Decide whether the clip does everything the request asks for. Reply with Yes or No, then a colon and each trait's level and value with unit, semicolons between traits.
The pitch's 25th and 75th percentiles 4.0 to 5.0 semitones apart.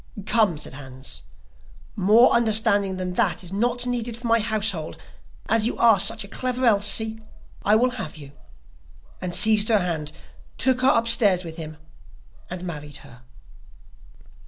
Yes: average, 4.6 semitones